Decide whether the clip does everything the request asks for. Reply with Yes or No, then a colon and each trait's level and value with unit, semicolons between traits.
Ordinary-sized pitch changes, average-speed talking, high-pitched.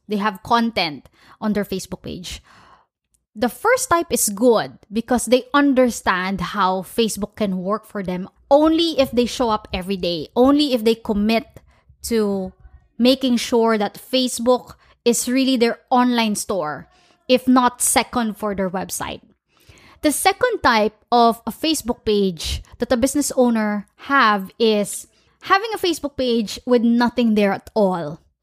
Yes: average, 3.7 semitones; average, 150 wpm; high, 235 Hz